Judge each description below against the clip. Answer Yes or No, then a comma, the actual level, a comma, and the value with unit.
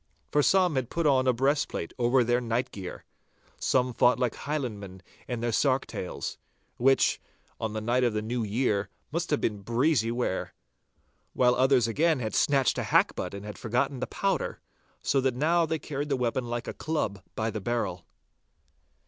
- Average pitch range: Yes, average, 3.7 semitones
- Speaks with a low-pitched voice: Yes, low, 125 Hz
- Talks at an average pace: Yes, average, 180 wpm